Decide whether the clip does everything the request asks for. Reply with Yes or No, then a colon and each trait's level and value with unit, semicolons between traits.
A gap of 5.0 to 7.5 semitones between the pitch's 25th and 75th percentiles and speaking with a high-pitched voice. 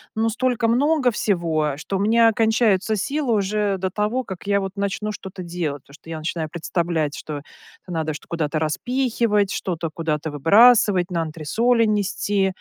Yes: average, 5.3 semitones; high, 195 Hz